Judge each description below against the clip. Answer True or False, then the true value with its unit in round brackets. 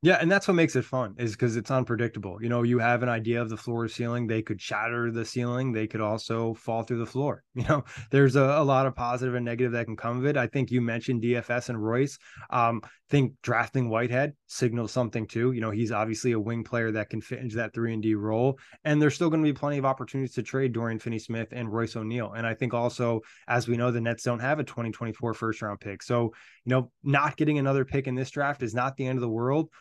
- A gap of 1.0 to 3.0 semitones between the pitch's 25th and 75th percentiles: True (2.4 semitones)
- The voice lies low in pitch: True (120 Hz)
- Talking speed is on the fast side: True (260 wpm)